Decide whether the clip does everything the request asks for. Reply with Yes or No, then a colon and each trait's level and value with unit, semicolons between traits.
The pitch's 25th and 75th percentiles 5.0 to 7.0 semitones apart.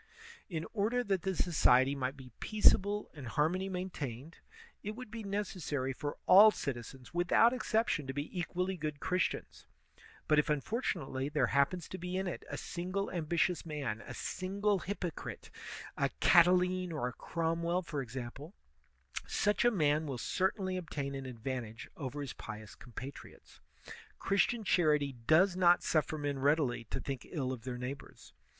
Yes: wide, 5.4 semitones